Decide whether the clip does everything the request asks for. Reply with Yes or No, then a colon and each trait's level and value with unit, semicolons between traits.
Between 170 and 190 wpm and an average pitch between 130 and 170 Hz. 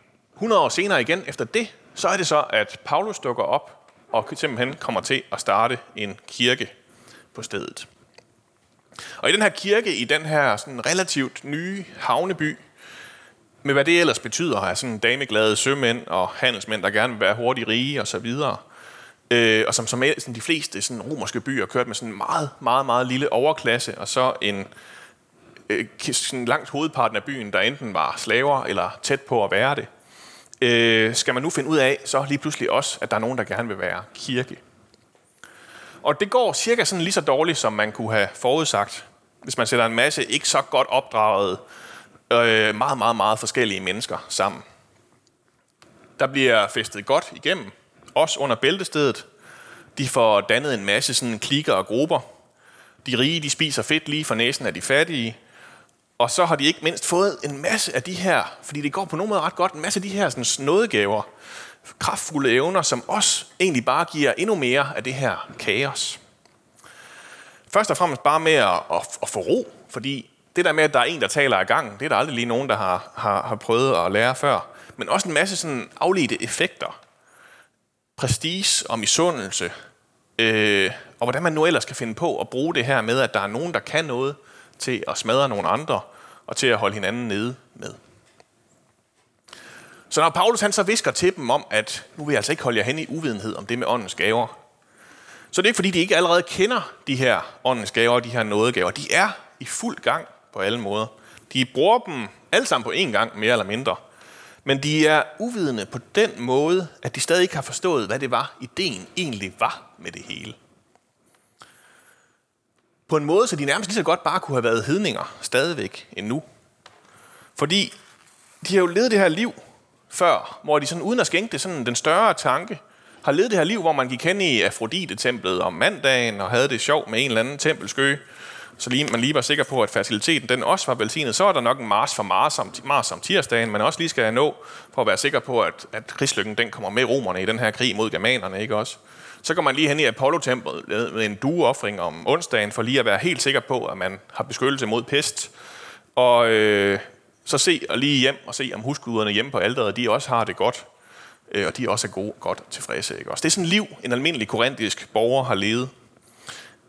No: average, 205 wpm; low, 135 Hz